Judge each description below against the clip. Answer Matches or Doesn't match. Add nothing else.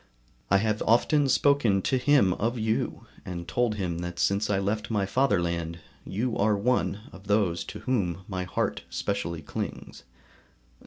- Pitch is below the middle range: Matches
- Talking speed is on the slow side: Doesn't match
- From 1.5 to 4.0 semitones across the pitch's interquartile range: Doesn't match